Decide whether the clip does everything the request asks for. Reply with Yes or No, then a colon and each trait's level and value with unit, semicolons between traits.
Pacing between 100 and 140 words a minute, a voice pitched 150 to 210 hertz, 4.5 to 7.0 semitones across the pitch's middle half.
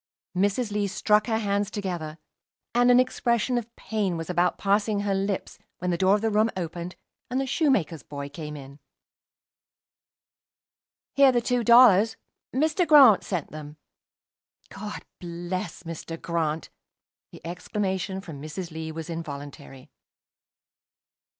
Yes: slow, 135 wpm; high, 190 Hz; average, 5.1 semitones